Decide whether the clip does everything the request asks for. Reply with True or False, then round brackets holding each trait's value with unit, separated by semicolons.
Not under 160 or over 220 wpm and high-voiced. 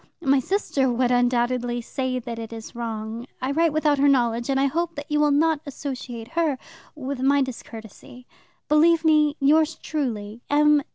True (170 wpm; 270 Hz)